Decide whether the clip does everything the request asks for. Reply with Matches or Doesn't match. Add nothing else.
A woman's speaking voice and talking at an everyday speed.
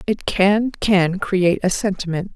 Matches